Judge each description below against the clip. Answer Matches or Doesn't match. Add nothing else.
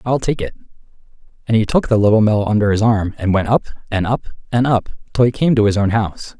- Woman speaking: Doesn't match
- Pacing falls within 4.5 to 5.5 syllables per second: Doesn't match